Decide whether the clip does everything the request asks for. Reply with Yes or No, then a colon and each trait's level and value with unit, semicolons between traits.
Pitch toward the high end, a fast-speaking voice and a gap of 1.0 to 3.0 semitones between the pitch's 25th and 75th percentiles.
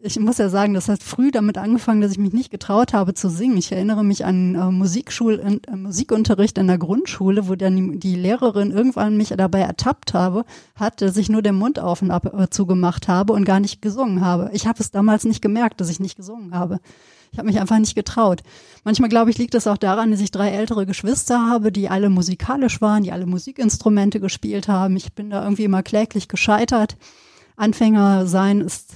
Yes: high, 205 Hz; fast, 215 wpm; narrow, 2.5 semitones